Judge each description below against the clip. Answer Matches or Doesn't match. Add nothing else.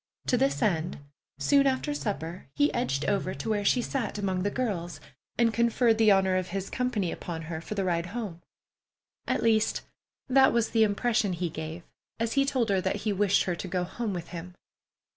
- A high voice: Matches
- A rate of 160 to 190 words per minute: Doesn't match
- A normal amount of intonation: Matches